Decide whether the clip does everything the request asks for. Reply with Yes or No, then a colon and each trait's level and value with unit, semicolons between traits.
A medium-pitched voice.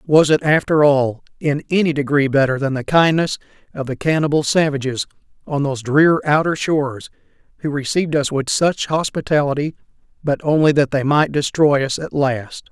Yes: medium, 145 Hz